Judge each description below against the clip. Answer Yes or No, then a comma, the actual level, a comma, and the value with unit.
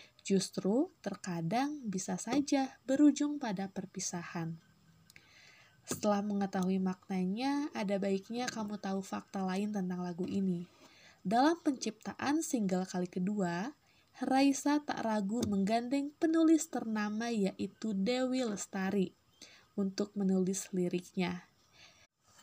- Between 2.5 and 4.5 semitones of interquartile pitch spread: No, average, 5.3 semitones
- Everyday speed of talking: No, slow, 95 wpm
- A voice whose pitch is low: No, high, 200 Hz